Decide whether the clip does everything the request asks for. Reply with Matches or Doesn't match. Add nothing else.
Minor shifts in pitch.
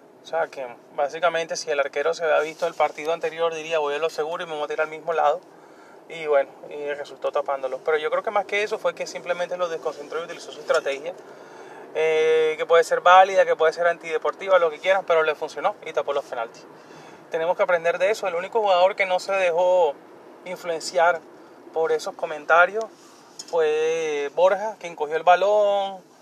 Doesn't match